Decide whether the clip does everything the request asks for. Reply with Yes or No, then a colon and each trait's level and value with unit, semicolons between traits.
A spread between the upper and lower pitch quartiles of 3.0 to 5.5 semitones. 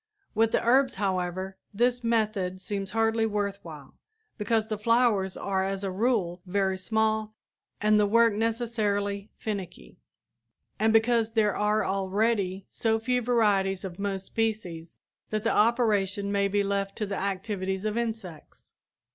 No: narrow, 2.6 semitones